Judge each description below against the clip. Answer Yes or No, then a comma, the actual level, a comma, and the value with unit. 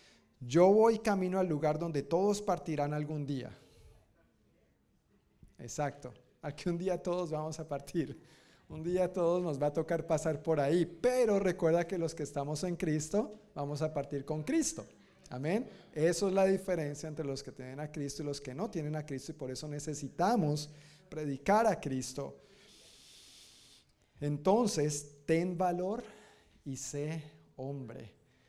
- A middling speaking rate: Yes, average, 150 wpm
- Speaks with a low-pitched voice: No, medium, 155 Hz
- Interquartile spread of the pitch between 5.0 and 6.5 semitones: No, average, 3.8 semitones